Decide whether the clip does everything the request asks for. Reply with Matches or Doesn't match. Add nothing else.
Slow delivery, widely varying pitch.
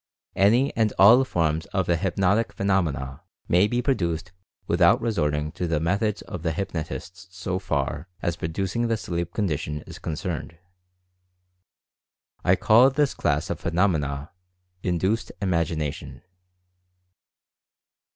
Doesn't match